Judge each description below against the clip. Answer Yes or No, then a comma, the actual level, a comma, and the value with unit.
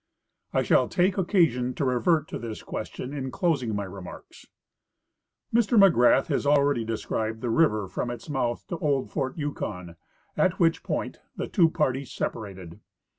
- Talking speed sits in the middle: Yes, average, 160 wpm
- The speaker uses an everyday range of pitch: No, wide, 6.4 semitones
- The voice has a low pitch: Yes, low, 130 Hz